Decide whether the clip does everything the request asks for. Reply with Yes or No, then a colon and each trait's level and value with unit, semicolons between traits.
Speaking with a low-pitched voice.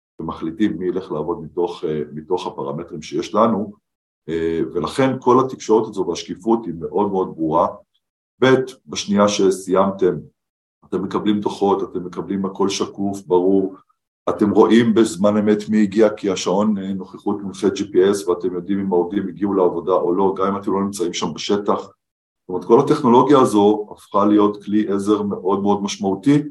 Yes: low, 100 Hz